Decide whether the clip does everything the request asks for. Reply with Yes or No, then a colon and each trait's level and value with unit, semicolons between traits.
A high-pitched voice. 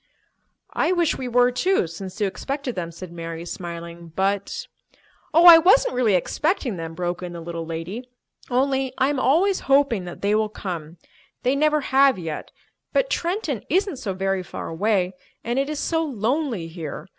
Yes: high, 220 Hz